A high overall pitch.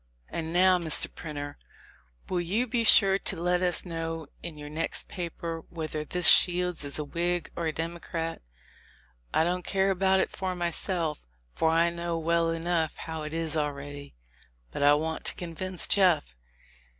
No: medium, 170 Hz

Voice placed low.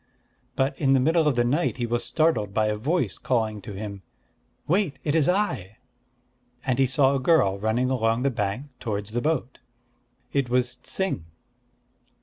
Yes: low, 125 Hz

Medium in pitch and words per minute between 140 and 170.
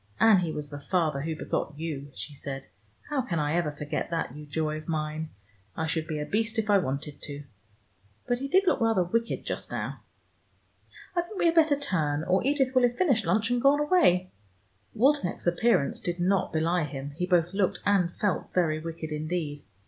No: medium, 175 Hz; average, 200 wpm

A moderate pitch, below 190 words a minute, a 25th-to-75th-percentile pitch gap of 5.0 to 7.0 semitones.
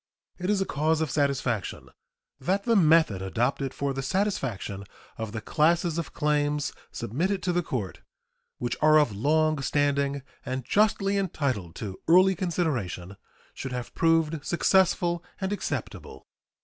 Yes: medium, 150 Hz; average, 140 wpm; wide, 5.5 semitones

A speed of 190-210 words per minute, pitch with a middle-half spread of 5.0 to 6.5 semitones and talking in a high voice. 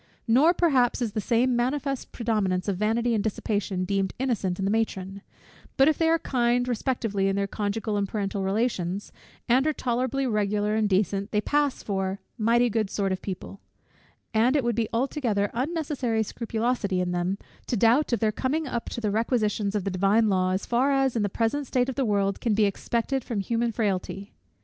No: average, 195 wpm; average, 3.7 semitones; high, 220 Hz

